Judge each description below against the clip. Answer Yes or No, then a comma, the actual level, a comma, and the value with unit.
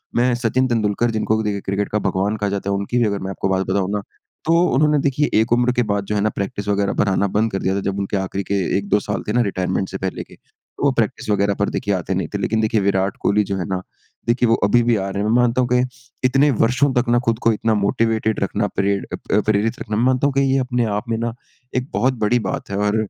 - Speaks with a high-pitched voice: No, low, 105 Hz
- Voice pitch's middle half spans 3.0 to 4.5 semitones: Yes, average, 3.3 semitones